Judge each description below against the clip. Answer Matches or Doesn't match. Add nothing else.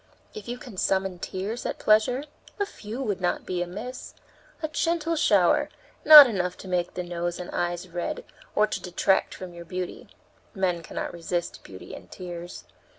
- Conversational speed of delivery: Matches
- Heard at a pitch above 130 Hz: Matches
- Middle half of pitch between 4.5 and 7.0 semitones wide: Matches